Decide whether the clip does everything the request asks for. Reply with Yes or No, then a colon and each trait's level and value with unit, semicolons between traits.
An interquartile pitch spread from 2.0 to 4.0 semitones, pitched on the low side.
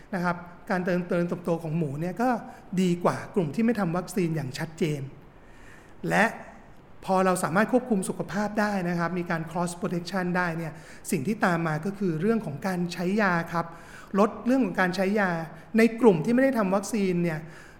No: average, 3.6 semitones; medium, 185 Hz